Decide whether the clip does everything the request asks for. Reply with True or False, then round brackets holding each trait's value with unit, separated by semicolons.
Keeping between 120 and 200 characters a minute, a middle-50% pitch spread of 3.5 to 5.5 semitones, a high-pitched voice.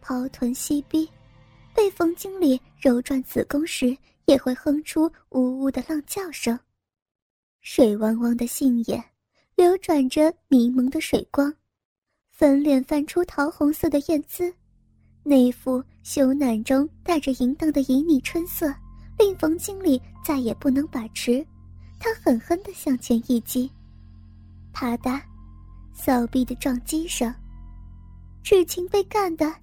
True (190 characters per minute; 4.2 semitones; 275 Hz)